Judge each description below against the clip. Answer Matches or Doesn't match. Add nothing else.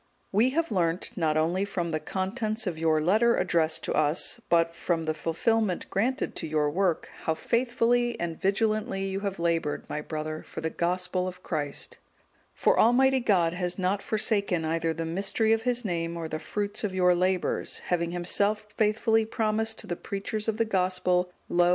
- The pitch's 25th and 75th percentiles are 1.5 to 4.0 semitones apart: Doesn't match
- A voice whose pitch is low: Doesn't match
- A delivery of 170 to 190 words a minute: Matches